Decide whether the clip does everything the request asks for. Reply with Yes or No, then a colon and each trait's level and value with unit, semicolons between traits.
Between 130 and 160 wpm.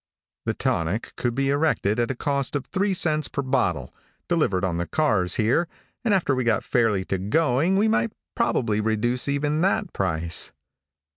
No: average, 170 wpm